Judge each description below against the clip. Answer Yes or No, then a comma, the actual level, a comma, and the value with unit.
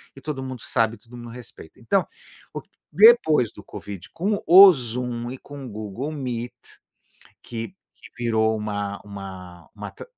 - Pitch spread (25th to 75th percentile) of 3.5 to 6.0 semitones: Yes, average, 4.2 semitones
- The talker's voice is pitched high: No, low, 120 Hz